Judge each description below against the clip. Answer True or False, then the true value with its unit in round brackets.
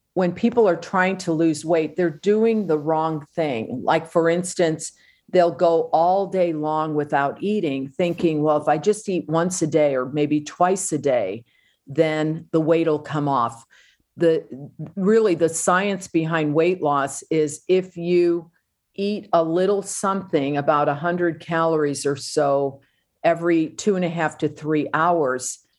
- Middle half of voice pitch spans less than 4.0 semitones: True (2.8 semitones)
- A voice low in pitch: False (165 Hz)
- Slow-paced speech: False (165 wpm)